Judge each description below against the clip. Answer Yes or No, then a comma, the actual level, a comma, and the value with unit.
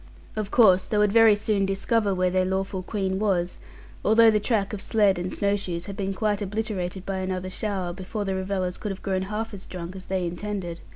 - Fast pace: Yes, fast, 215 wpm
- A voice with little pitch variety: Yes, narrow, 2.0 semitones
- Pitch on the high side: Yes, high, 195 Hz